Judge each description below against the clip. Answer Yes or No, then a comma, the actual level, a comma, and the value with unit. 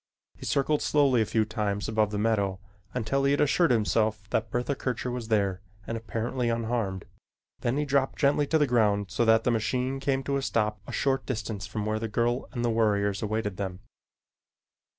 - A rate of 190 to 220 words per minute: Yes, average, 195 wpm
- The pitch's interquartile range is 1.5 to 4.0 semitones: Yes, average, 3.6 semitones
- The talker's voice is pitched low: Yes, low, 115 Hz